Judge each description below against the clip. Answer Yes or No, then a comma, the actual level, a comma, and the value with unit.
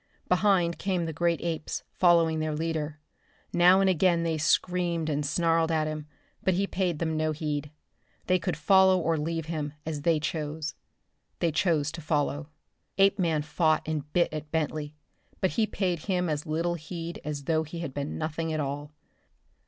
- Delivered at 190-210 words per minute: No, average, 175 wpm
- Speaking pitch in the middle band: Yes, medium, 160 Hz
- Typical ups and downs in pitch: No, narrow, 2.2 semitones